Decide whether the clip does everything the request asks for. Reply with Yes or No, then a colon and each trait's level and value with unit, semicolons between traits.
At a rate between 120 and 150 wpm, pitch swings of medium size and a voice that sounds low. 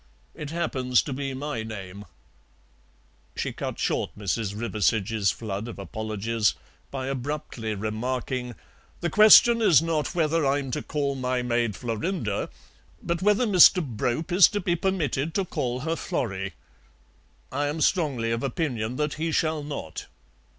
No: average, 145 wpm; wide, 6.0 semitones; low, 130 Hz